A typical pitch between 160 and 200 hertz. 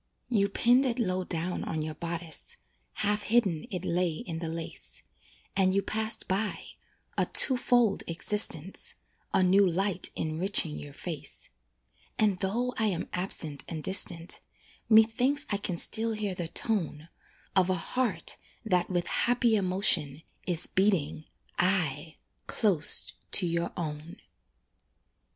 Yes: medium, 185 Hz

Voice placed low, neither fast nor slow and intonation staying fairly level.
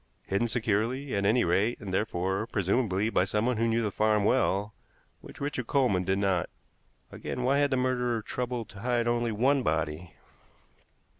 No: low, 110 Hz; average, 165 wpm; average, 4.0 semitones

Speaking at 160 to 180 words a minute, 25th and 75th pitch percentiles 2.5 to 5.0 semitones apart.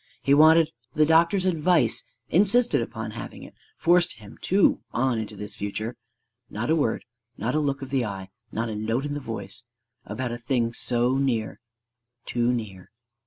No: average, 170 wpm; wide, 5.5 semitones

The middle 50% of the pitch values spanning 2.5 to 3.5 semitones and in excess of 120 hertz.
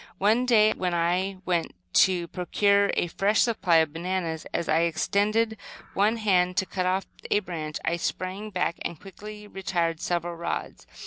Yes: average, 3.2 semitones; medium, 185 Hz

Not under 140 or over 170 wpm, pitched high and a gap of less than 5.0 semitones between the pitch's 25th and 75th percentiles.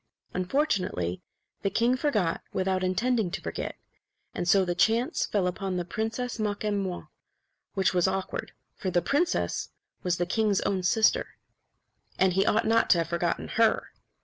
Yes: average, 150 wpm; high, 195 Hz; average, 3.6 semitones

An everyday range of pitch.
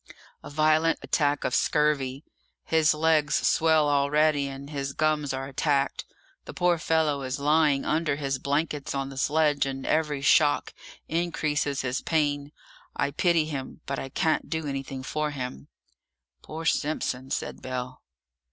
No: narrow, 2.2 semitones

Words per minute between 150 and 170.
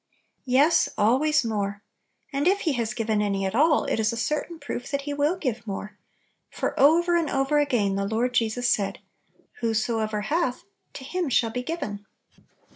No: average, 185 wpm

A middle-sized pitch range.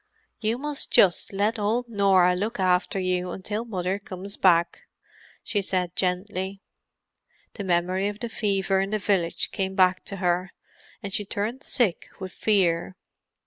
No: narrow, 2.3 semitones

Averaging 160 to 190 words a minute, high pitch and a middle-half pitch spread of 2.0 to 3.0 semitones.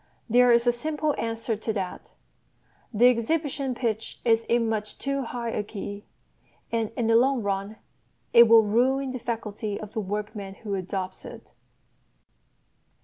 No: average, 150 wpm; high, 225 Hz; average, 2.7 semitones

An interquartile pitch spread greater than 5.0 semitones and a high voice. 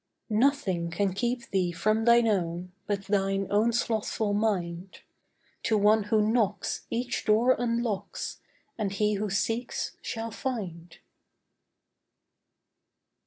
No: average, 2.9 semitones; high, 210 Hz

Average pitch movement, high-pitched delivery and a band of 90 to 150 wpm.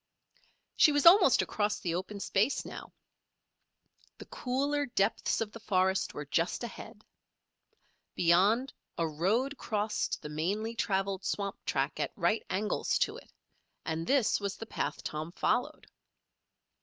Yes: average, 4.5 semitones; high, 205 Hz; slow, 135 wpm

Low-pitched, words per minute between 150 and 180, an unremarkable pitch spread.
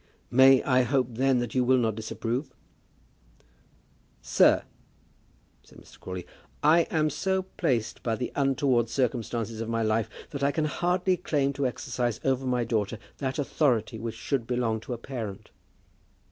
Yes: low, 125 Hz; average, 160 wpm; average, 3.5 semitones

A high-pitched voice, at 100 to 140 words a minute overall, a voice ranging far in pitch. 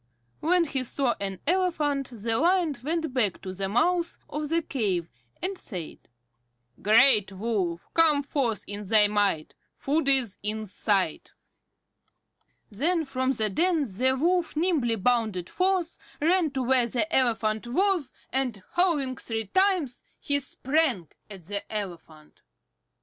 Yes: very high, 255 Hz; slow, 135 wpm; wide, 7.4 semitones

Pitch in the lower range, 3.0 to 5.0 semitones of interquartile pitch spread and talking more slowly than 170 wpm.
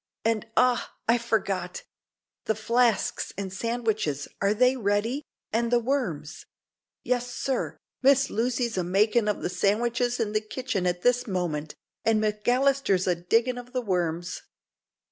No: high, 225 Hz; average, 4.2 semitones; average, 145 wpm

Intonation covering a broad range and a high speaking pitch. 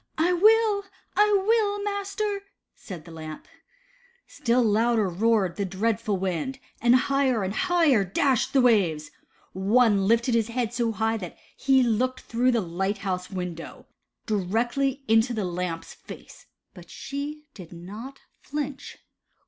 Yes: wide, 6.1 semitones; high, 230 Hz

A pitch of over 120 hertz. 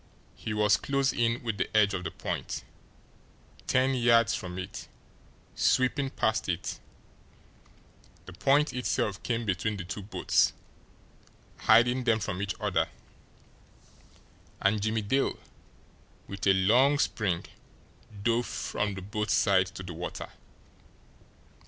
No: low, 110 Hz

